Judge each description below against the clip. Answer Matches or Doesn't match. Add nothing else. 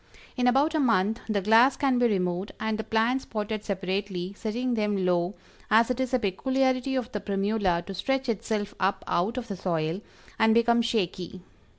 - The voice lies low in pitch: Doesn't match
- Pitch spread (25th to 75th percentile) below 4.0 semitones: Doesn't match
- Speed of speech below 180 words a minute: Doesn't match